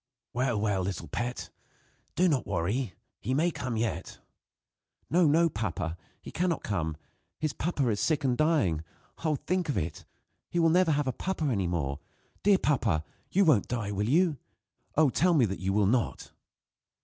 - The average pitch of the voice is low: Yes, low, 130 Hz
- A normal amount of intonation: No, wide, 8.0 semitones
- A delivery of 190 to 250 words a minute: No, average, 175 wpm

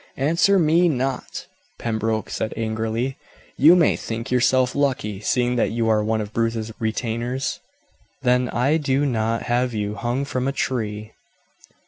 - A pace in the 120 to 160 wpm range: Yes, average, 145 wpm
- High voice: No, low, 120 Hz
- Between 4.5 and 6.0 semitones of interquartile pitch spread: No, average, 3.3 semitones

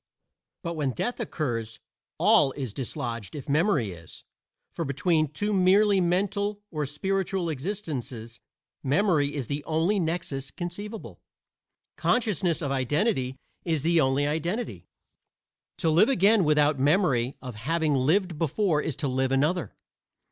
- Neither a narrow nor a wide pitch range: No, wide, 5.7 semitones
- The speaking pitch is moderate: Yes, medium, 155 Hz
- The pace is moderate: No, slow, 130 wpm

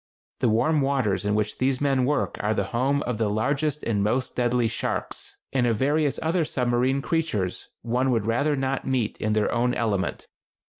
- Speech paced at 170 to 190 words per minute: Yes, average, 185 wpm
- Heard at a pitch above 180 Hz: No, low, 125 Hz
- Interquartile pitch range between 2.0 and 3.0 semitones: No, average, 4.0 semitones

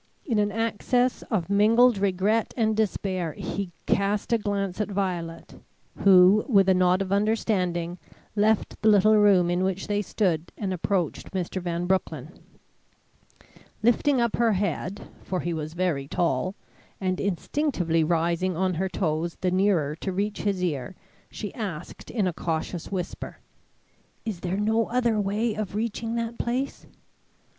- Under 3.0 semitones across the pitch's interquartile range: No, average, 3.3 semitones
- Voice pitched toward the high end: Yes, high, 195 Hz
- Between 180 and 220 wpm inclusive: No, average, 150 wpm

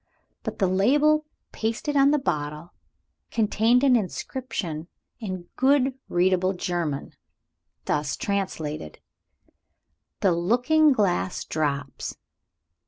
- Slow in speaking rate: Yes, slow, 95 wpm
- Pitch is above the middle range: Yes, high, 195 Hz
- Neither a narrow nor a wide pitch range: No, wide, 7.0 semitones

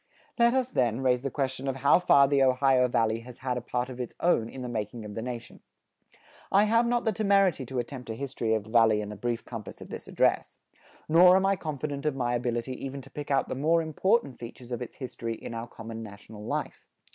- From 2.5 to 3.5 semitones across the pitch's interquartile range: No, average, 4.1 semitones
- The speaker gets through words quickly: Yes, fast, 235 wpm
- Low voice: Yes, low, 130 Hz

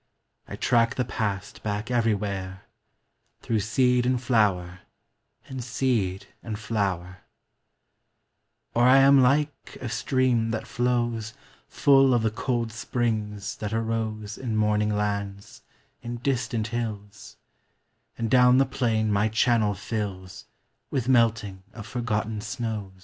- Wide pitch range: No, average, 2.8 semitones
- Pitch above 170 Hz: No, low, 110 Hz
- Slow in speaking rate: Yes, slow, 120 wpm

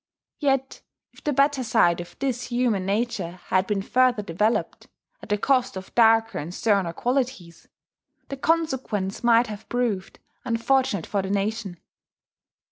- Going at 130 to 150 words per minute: Yes, average, 140 wpm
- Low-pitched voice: No, high, 225 Hz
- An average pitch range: Yes, average, 4.7 semitones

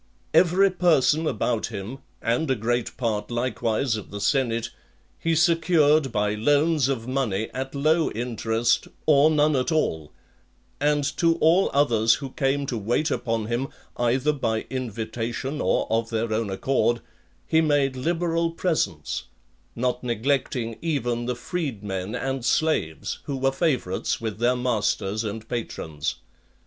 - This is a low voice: Yes, low, 125 Hz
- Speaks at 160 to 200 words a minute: No, average, 140 wpm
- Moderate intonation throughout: Yes, average, 4.8 semitones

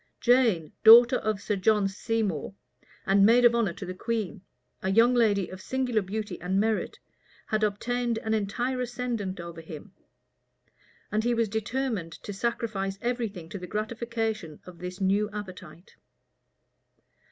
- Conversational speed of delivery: Yes, average, 150 wpm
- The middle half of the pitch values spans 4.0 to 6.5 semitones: No, average, 3.5 semitones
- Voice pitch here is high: Yes, high, 215 Hz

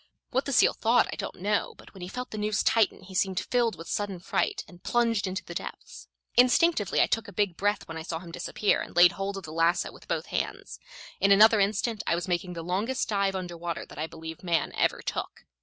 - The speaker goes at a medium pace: No, fast, 240 wpm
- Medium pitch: No, high, 195 Hz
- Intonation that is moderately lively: Yes, average, 3.9 semitones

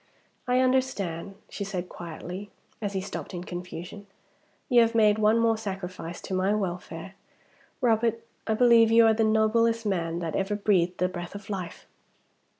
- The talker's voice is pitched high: Yes, high, 205 Hz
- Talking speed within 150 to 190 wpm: Yes, average, 160 wpm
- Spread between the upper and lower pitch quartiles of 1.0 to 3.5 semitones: No, average, 3.9 semitones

